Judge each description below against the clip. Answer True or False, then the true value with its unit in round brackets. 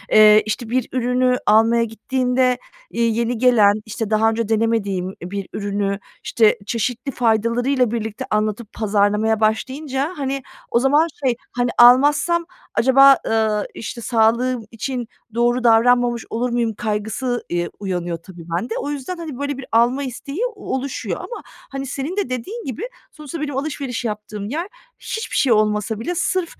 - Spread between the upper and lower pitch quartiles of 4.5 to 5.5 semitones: False (3.5 semitones)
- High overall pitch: True (235 Hz)